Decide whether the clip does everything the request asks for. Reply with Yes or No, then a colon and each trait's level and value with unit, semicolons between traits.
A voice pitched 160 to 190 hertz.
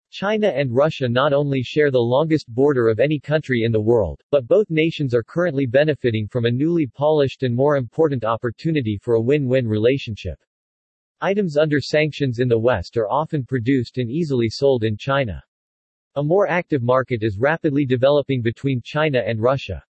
No: low, 135 Hz